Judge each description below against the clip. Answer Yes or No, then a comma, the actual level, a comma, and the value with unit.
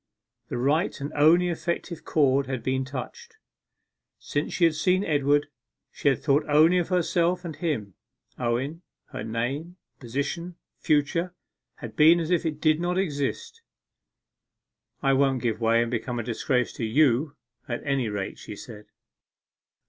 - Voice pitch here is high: No, medium, 145 Hz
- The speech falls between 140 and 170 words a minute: Yes, average, 150 wpm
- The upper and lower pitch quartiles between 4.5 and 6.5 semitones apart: Yes, average, 5.0 semitones